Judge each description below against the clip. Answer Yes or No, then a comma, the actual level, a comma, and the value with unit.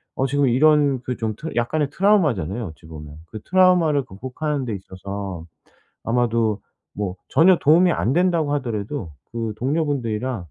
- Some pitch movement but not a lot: No, wide, 6.2 semitones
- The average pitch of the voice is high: No, low, 125 Hz